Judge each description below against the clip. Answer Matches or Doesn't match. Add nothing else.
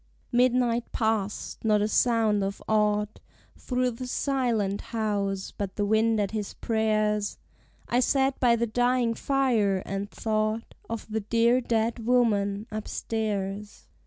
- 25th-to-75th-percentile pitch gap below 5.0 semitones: Matches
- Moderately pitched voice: Doesn't match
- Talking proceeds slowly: Matches